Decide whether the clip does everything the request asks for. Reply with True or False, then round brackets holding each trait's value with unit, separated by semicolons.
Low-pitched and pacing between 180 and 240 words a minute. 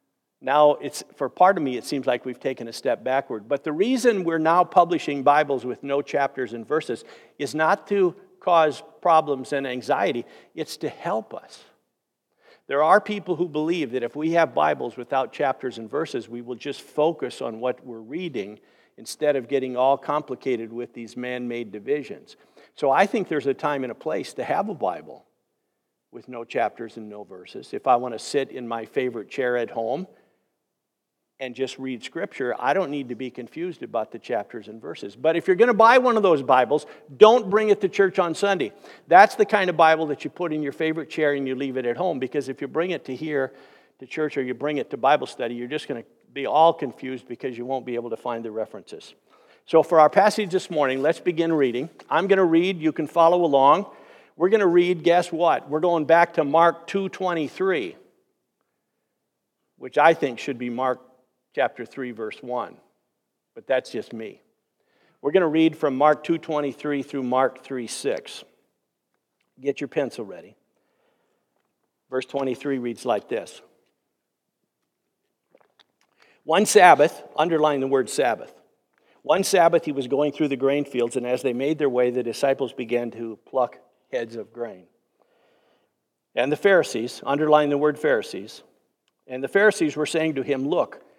False (145 Hz; 190 wpm)